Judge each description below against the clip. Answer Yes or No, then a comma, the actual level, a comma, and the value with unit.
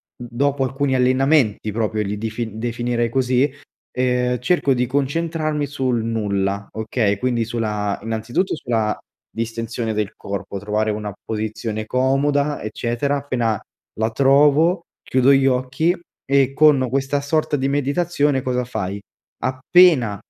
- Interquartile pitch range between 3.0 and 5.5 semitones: Yes, average, 4.0 semitones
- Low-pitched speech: Yes, low, 125 Hz